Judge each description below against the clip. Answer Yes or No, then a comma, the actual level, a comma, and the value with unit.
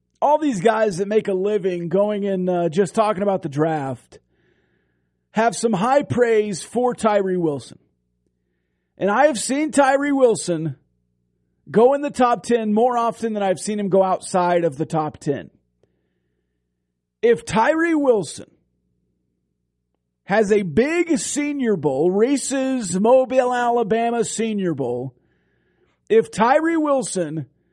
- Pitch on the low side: No, high, 200 Hz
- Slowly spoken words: Yes, slow, 130 wpm